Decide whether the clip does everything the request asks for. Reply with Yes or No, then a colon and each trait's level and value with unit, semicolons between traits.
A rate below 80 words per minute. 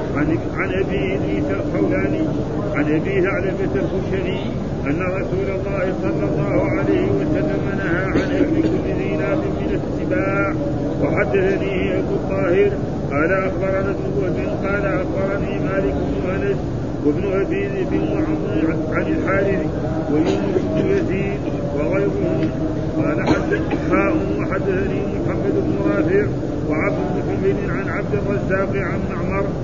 No: average, 110 wpm